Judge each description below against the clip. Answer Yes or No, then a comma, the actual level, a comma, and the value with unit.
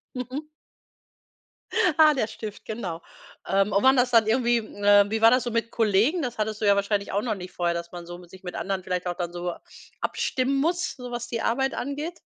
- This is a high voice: Yes, high, 220 Hz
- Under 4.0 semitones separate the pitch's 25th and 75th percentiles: No, average, 4.6 semitones